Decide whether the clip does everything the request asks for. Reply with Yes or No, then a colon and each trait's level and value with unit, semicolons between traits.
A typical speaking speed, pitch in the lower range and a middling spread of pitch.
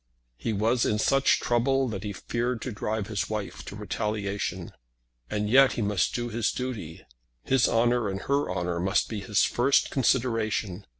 Yes: average, 170 wpm; low, 110 Hz; average, 3.2 semitones